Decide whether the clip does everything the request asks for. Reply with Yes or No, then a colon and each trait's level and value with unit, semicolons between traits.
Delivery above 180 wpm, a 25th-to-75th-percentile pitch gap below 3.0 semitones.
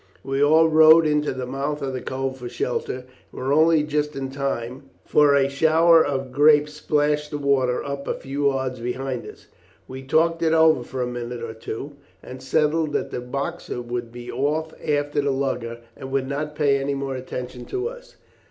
Yes: average, 195 wpm; narrow, 2.5 semitones